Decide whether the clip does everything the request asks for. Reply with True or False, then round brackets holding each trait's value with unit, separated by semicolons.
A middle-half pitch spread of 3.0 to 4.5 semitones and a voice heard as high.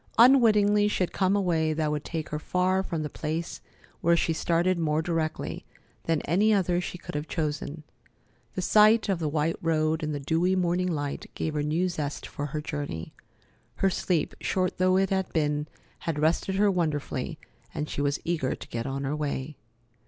False (3.5 semitones; 165 Hz)